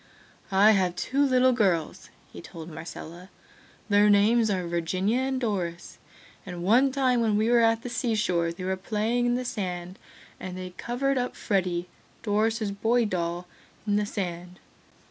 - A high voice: Yes, high, 205 Hz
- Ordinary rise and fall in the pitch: Yes, average, 4.8 semitones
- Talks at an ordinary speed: Yes, average, 165 wpm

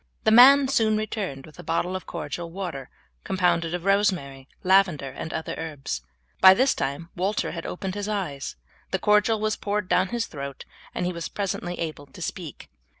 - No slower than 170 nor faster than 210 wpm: Yes, average, 180 wpm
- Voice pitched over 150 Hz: Yes, medium, 185 Hz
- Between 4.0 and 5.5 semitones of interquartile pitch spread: Yes, average, 4.5 semitones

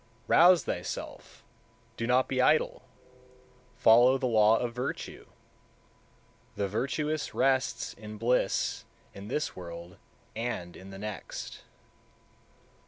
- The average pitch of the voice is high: No, low, 115 Hz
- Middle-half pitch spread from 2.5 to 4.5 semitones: Yes, average, 3.9 semitones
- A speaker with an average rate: No, slow, 110 wpm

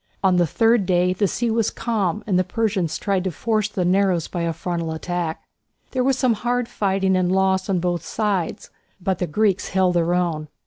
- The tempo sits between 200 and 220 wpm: Yes, fast, 205 wpm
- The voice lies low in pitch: No, high, 190 Hz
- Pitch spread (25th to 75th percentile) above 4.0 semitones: No, average, 3.2 semitones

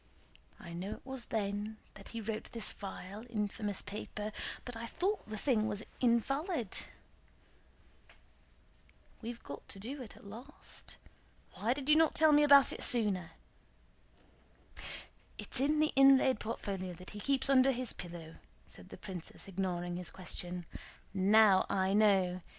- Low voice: No, high, 215 Hz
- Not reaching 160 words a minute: Yes, average, 140 wpm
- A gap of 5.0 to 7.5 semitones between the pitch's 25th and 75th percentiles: Yes, wide, 5.4 semitones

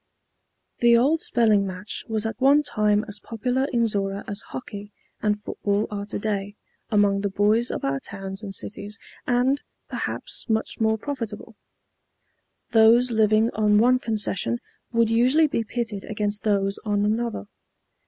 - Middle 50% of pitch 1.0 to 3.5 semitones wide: Yes, narrow, 2.4 semitones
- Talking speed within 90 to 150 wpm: Yes, average, 145 wpm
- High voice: Yes, high, 215 Hz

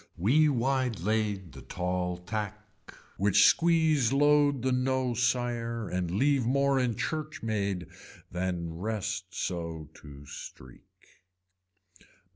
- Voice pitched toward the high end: No, low, 110 Hz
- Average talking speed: No, slow, 110 wpm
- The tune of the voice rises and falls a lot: Yes, wide, 6.3 semitones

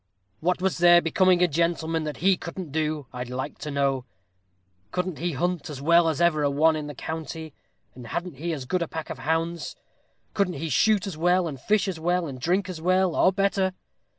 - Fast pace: Yes, fast, 210 wpm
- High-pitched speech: No, medium, 165 Hz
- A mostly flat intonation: No, average, 3.1 semitones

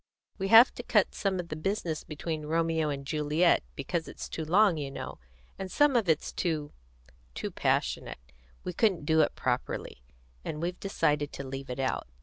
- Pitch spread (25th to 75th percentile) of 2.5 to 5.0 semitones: Yes, average, 3.7 semitones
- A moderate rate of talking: Yes, average, 180 wpm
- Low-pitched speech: No, medium, 160 Hz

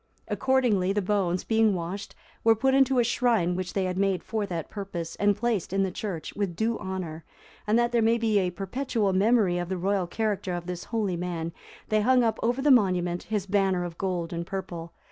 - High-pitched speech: Yes, high, 195 Hz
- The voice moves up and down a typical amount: Yes, average, 4.0 semitones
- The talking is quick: Yes, fast, 210 wpm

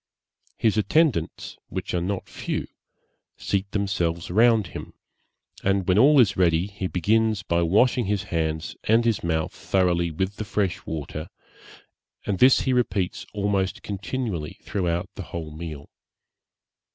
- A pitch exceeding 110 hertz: No, very low, 95 Hz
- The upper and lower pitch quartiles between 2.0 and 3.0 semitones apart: No, average, 3.9 semitones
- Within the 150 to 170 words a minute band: No, average, 140 wpm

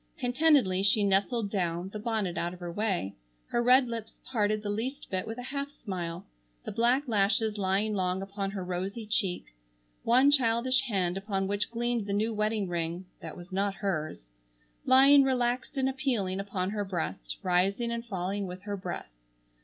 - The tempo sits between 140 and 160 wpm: No, average, 170 wpm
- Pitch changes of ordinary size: Yes, average, 4.3 semitones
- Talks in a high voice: Yes, high, 205 Hz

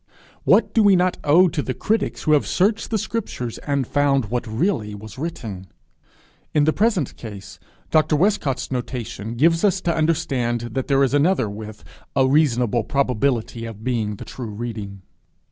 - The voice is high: No, low, 135 Hz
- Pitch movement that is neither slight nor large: No, wide, 6.0 semitones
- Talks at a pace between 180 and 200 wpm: No, average, 165 wpm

